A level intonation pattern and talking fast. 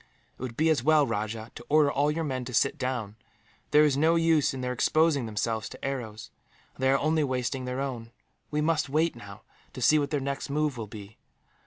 No: average, 4.3 semitones; fast, 225 wpm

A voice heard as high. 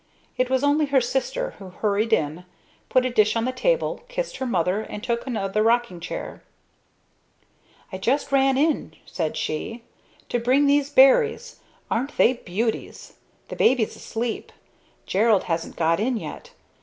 Yes: high, 240 Hz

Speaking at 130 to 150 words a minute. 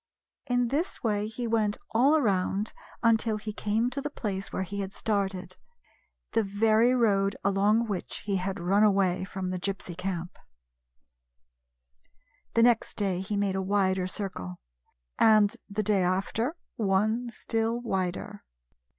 Yes: average, 145 wpm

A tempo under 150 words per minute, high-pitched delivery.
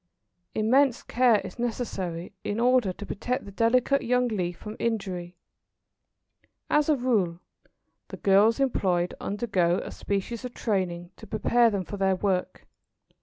Yes: average, 140 wpm; high, 210 Hz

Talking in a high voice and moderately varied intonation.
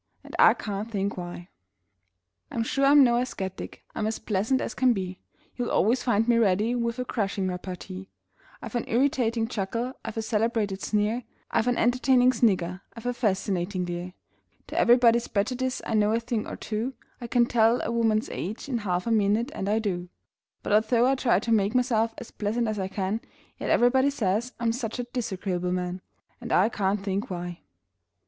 Yes: high, 220 Hz; average, 3.6 semitones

